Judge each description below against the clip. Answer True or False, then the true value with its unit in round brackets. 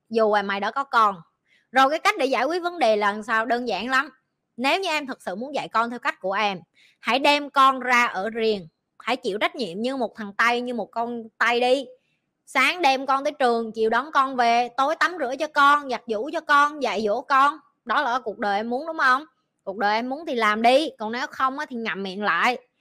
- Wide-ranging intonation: False (3.9 semitones)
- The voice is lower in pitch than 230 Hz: False (245 Hz)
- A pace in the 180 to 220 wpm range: False (245 wpm)